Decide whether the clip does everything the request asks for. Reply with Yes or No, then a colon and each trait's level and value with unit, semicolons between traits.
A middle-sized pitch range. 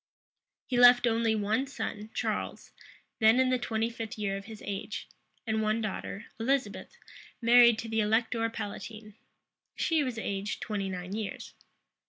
No: narrow, 2.2 semitones